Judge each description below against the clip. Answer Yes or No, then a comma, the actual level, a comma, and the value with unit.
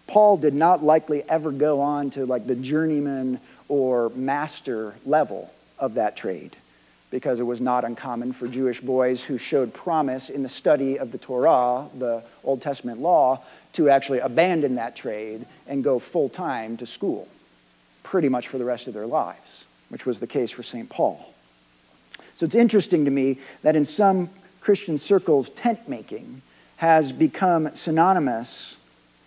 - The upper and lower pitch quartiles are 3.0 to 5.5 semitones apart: Yes, average, 4.1 semitones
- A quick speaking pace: No, average, 160 wpm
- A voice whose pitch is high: No, low, 135 Hz